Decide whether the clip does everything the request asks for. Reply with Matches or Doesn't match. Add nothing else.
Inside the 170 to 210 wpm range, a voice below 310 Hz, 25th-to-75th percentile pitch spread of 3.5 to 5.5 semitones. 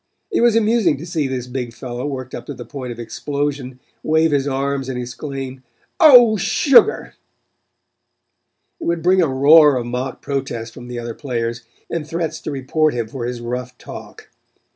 Matches